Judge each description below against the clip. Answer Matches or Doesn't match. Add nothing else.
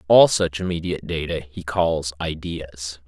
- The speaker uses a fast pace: Doesn't match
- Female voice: Doesn't match